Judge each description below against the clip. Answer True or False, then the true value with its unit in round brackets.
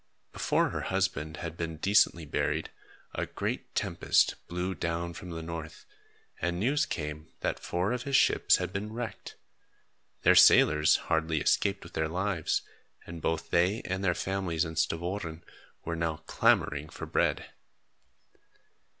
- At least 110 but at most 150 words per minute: True (145 wpm)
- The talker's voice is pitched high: False (85 Hz)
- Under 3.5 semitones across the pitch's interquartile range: True (3.0 semitones)